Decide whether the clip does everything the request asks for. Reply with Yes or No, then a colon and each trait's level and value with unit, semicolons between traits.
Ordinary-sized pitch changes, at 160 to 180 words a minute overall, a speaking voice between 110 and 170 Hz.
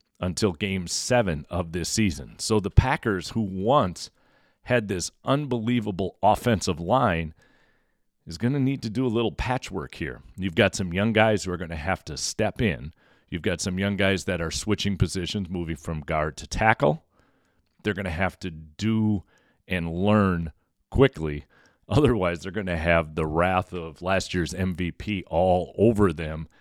No: average, 4.1 semitones; average, 170 wpm; very low, 95 Hz